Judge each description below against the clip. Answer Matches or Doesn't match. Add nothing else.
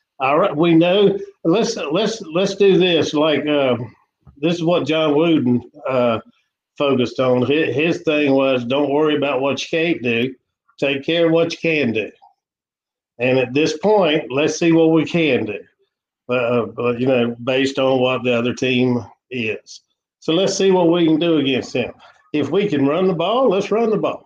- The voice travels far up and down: Doesn't match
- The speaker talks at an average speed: Matches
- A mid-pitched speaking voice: Matches